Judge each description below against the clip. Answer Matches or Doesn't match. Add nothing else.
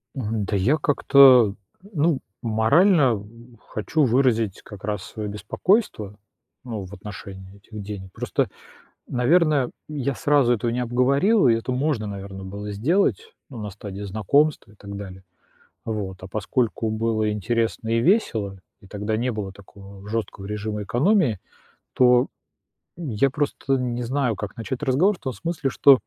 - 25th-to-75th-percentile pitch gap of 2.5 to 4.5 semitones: Doesn't match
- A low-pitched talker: Matches